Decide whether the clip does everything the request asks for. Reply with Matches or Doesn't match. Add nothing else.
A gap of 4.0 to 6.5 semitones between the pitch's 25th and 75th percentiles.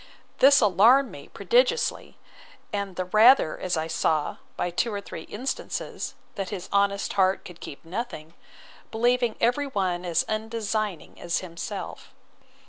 Matches